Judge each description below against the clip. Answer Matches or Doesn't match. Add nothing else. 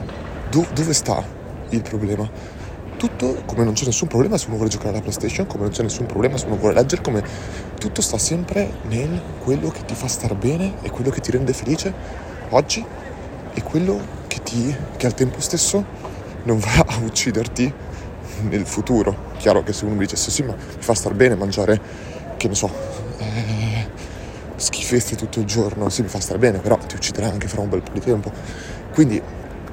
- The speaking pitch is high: Doesn't match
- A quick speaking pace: Matches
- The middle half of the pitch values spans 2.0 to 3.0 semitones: Doesn't match